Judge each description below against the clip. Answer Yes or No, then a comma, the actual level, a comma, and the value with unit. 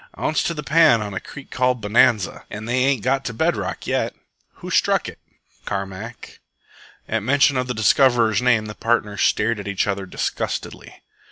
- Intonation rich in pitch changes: No, average, 3.9 semitones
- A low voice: Yes, low, 115 Hz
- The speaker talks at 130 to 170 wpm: No, average, 180 wpm